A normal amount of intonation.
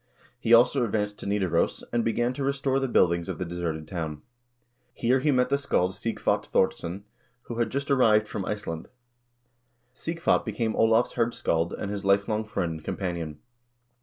No: wide, 5.7 semitones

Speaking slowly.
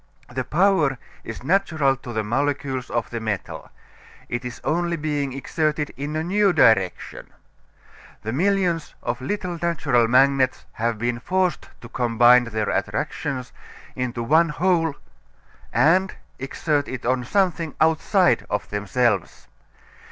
Yes: slow, 130 wpm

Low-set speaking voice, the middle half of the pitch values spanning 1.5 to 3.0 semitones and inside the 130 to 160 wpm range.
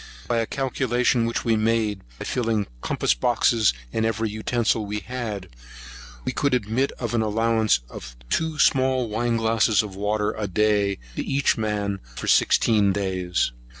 Yes: low, 110 Hz; narrow, 2.4 semitones; average, 155 wpm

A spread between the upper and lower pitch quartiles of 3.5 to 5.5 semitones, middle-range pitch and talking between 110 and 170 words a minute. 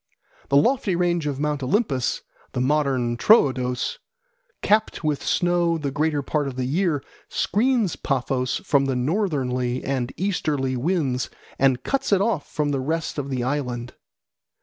Yes: average, 5.0 semitones; medium, 145 Hz; average, 150 wpm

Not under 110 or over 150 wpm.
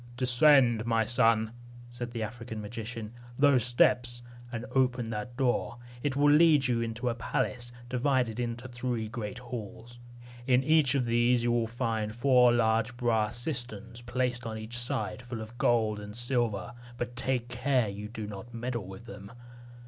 No: average, 165 wpm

